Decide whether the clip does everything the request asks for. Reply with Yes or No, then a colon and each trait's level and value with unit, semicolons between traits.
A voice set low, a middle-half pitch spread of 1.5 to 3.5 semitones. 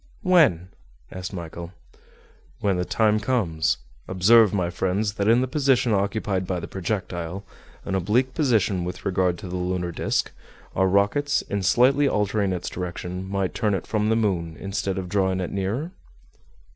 Yes: very low, 95 Hz; average, 3.2 semitones